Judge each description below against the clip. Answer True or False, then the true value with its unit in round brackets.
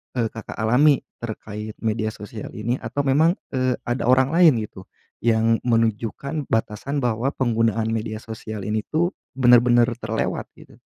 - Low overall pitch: True (115 Hz)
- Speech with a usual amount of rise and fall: True (3.0 semitones)